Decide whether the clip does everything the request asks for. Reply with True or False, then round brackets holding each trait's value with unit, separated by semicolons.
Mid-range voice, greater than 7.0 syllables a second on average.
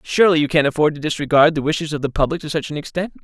True (155 Hz; 7.5 syllables/s)